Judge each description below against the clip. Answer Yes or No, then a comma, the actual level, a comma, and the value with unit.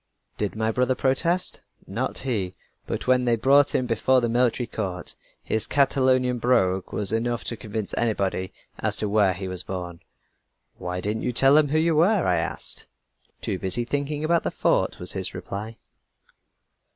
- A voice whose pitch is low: Yes, low, 120 Hz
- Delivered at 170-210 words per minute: Yes, average, 175 wpm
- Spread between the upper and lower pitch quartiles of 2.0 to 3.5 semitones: No, average, 4.9 semitones